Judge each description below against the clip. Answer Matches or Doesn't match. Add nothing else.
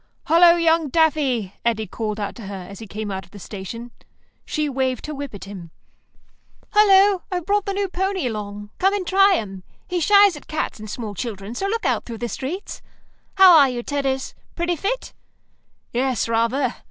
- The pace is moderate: Matches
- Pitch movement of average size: Doesn't match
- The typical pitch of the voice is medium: Doesn't match